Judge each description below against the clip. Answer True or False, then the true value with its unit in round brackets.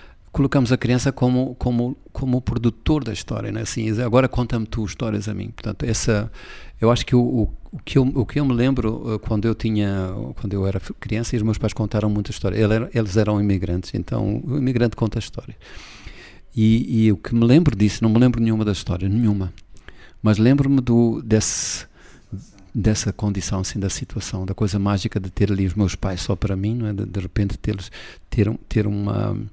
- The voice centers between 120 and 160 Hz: False (110 Hz)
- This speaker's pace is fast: True (205 wpm)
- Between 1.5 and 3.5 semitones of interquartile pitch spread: True (2.8 semitones)